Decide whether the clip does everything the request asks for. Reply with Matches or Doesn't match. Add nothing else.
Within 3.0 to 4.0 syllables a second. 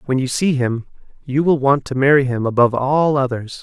Doesn't match